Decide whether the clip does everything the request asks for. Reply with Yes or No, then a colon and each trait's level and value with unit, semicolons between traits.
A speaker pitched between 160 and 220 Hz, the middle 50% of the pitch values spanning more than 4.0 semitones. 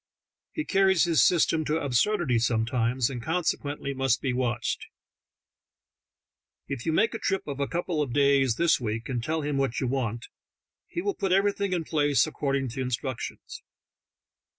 No: medium, 140 Hz; average, 5.2 semitones